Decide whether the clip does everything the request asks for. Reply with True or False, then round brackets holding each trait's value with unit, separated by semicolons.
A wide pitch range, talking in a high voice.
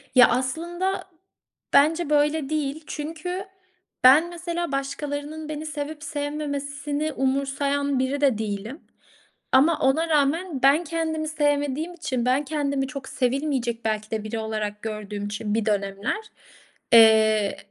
False (3.9 semitones; 285 Hz)